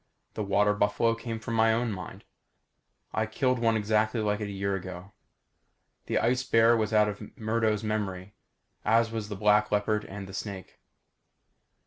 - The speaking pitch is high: No, low, 105 Hz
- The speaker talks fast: No, average, 165 wpm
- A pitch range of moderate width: No, narrow, 1.7 semitones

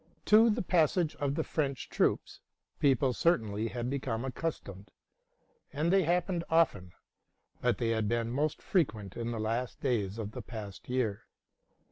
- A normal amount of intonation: No, wide, 6.3 semitones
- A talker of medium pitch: No, low, 125 Hz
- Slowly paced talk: No, average, 155 wpm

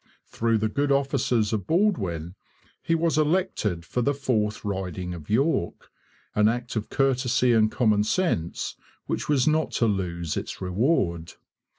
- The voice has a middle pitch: No, low, 115 Hz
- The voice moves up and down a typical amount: No, wide, 6.6 semitones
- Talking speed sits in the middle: Yes, average, 150 wpm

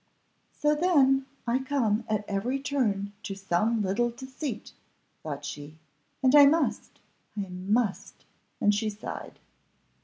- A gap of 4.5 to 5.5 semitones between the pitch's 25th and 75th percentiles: Yes, average, 5.2 semitones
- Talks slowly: Yes, slow, 125 wpm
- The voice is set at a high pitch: Yes, high, 225 Hz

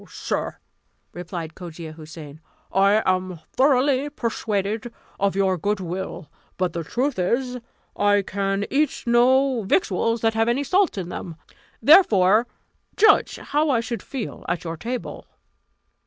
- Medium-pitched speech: No, high, 205 Hz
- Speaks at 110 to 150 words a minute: Yes, slow, 135 wpm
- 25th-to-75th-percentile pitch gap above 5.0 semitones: Yes, wide, 5.5 semitones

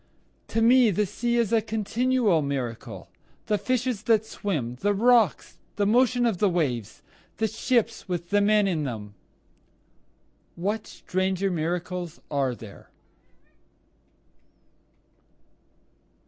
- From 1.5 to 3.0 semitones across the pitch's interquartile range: No, wide, 5.5 semitones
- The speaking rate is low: Yes, slow, 115 wpm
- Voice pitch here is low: No, high, 200 Hz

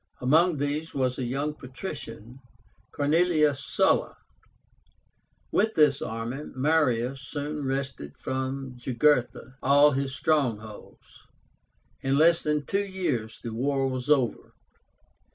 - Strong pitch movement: No, average, 3.0 semitones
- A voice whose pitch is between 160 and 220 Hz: No, low, 135 Hz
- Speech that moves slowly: Yes, slow, 110 wpm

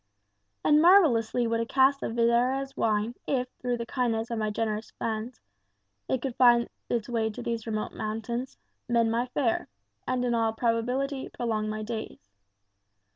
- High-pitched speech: Yes, high, 235 Hz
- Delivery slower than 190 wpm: Yes, average, 160 wpm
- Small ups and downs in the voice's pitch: Yes, narrow, 2.1 semitones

